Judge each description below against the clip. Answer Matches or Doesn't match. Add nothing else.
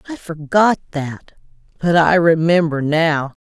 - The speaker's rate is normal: Doesn't match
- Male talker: Doesn't match